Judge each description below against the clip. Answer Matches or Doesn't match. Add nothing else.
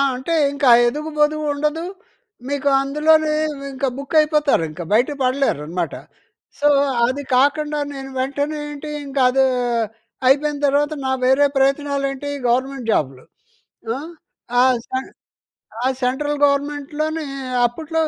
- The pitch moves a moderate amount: Doesn't match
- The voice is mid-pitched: Doesn't match